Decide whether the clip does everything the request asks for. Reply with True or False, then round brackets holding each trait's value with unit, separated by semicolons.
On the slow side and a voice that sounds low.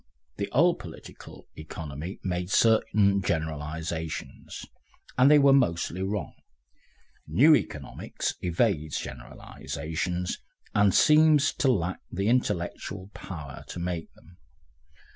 True (105 wpm; 90 Hz)